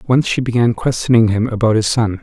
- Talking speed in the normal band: No, fast, 215 wpm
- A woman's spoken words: No, male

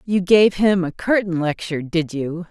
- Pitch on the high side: No, medium, 180 Hz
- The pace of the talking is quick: No, average, 190 wpm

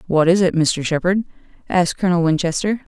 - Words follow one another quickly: No, average, 165 wpm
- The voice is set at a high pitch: No, medium, 175 Hz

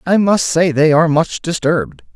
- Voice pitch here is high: No, medium, 160 Hz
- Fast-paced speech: No, average, 195 wpm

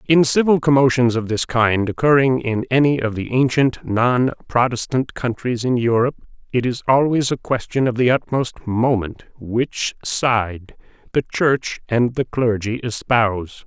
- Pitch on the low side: Yes, low, 125 Hz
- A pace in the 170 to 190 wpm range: No, average, 150 wpm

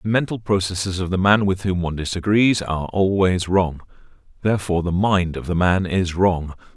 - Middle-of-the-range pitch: No, very low, 95 Hz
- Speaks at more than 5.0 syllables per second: Yes, 5.4 syllables/s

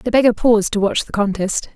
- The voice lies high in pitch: Yes, high, 215 Hz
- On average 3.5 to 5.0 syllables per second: No, 6.0 syllables/s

